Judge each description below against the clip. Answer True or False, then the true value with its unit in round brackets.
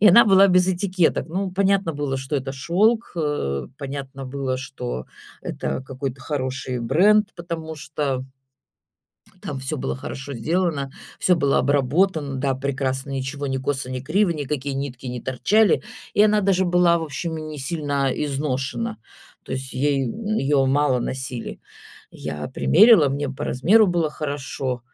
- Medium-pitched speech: True (145 Hz)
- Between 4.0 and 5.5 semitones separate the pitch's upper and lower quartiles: True (4.7 semitones)